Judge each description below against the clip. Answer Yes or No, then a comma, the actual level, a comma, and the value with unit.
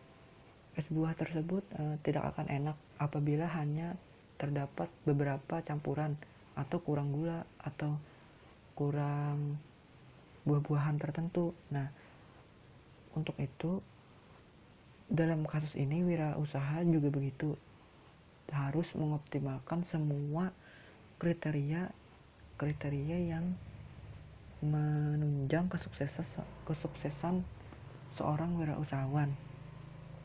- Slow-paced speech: Yes, slow, 75 wpm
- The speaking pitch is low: No, medium, 150 Hz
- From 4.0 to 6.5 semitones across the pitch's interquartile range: No, narrow, 2.4 semitones